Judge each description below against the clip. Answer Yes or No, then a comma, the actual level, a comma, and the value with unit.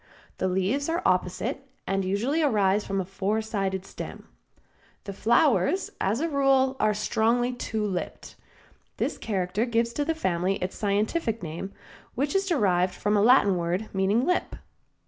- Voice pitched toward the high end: Yes, high, 210 Hz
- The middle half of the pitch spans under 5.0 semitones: No, wide, 5.4 semitones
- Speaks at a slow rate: No, average, 155 wpm